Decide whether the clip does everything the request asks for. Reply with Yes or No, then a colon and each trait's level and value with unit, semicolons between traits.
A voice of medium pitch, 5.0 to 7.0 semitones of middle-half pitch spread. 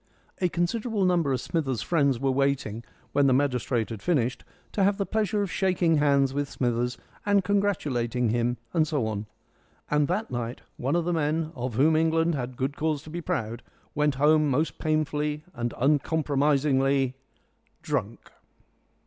No: medium, 145 Hz; average, 4.3 semitones